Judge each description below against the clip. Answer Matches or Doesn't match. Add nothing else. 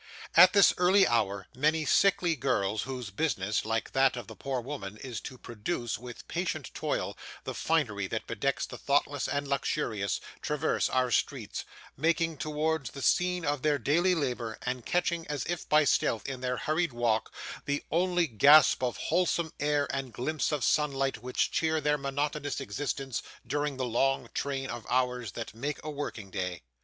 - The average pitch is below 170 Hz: Matches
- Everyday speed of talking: Matches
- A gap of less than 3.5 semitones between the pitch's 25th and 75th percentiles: Doesn't match